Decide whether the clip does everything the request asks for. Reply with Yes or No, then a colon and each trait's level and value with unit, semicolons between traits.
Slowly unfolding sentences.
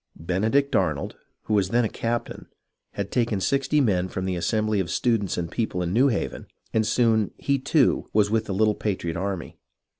No: average, 190 wpm